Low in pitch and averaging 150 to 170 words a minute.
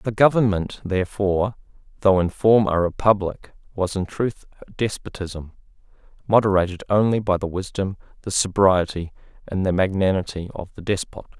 No: very low, 95 Hz; slow, 135 wpm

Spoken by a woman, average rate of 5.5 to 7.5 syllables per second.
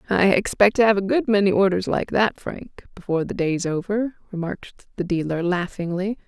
Yes: female; 5.6 syllables/s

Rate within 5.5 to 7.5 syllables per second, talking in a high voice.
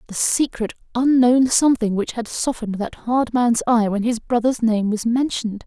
No: 5.0 syllables/s; high, 235 Hz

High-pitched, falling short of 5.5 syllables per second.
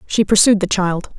Yes: high, 195 Hz; 5.0 syllables/s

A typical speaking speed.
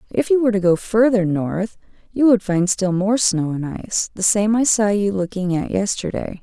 No: fast, 215 wpm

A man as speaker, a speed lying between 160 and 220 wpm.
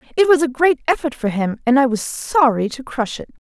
No: female; fast, 205 wpm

